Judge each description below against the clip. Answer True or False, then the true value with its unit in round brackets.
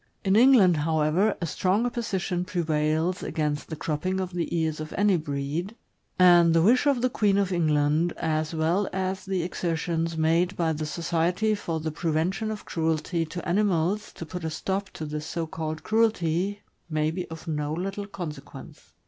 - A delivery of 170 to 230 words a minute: True (175 wpm)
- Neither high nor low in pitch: True (170 Hz)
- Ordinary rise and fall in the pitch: True (3.3 semitones)